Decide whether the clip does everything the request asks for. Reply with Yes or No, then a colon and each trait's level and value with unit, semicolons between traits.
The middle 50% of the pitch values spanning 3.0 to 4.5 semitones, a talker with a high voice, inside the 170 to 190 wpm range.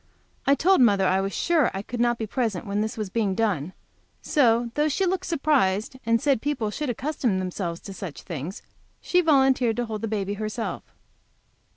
No: wide, 5.5 semitones; high, 225 Hz; average, 185 wpm